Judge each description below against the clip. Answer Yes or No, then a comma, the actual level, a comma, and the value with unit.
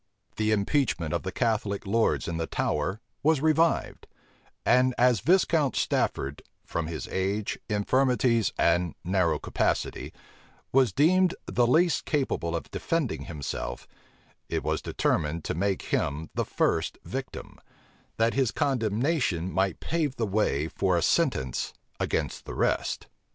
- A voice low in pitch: Yes, low, 110 Hz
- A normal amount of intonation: No, wide, 8.0 semitones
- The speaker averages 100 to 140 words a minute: Yes, slow, 135 wpm